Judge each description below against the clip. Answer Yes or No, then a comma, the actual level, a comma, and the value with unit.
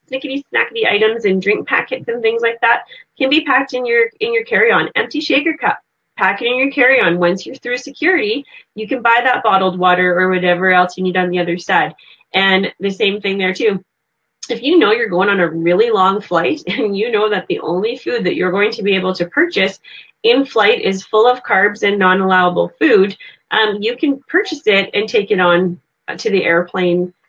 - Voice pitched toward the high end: Yes, high, 210 Hz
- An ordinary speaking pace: No, fast, 220 wpm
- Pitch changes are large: Yes, wide, 6.9 semitones